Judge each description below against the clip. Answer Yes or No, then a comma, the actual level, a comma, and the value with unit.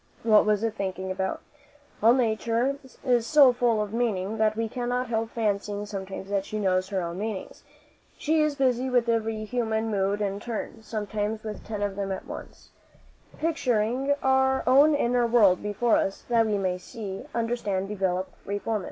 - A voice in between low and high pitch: No, high, 220 Hz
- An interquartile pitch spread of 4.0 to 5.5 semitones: No, average, 3.2 semitones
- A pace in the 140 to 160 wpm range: No, average, 175 wpm